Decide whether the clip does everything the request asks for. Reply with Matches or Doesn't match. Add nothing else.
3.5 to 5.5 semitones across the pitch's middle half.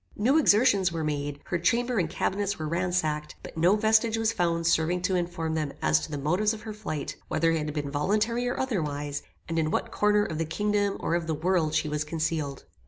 Matches